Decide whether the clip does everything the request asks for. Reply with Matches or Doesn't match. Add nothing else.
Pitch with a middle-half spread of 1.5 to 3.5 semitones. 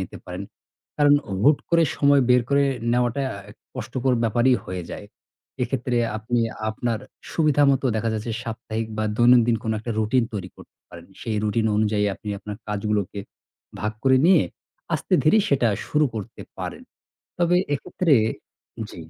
Doesn't match